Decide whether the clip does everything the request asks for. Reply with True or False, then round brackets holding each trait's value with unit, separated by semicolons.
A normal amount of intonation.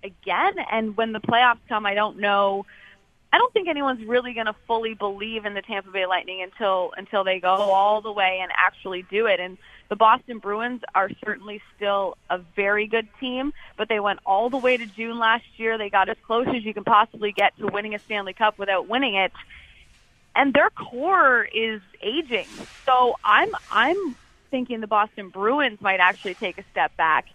True (3.3 semitones)